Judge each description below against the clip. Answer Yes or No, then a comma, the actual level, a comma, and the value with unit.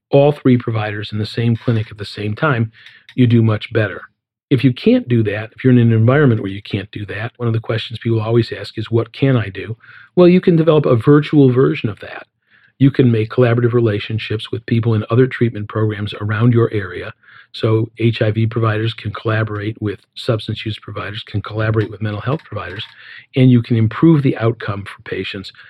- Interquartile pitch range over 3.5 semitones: No, average, 2.8 semitones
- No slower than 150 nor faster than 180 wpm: No, fast, 205 wpm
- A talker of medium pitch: No, low, 115 Hz